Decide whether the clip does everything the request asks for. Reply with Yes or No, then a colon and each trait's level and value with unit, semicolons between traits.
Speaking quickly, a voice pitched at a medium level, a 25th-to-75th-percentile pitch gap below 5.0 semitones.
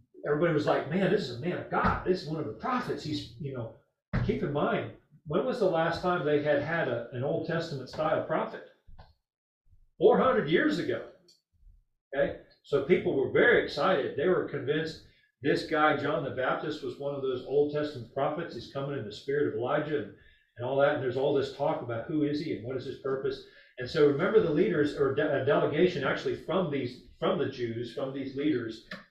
No: fast, 210 wpm; medium, 150 Hz; average, 5.3 semitones